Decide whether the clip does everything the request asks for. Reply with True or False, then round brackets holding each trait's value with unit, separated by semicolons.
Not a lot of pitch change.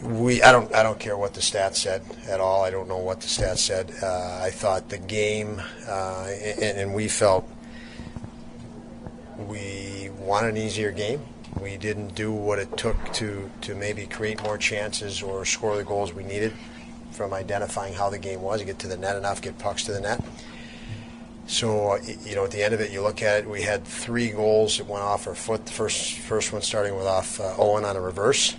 True (1.6 semitones)